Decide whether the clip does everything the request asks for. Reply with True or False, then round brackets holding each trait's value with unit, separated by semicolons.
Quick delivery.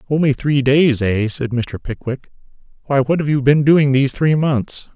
False (195 wpm)